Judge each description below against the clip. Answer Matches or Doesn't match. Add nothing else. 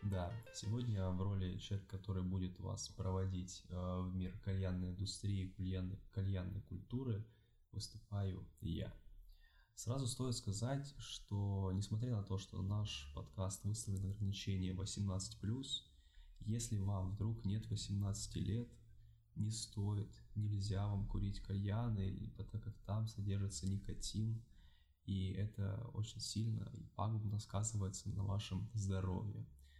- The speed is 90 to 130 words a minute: Matches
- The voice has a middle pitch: Doesn't match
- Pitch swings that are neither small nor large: Doesn't match